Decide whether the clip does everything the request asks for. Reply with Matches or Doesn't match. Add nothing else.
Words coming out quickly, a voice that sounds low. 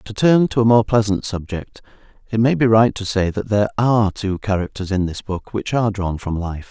Matches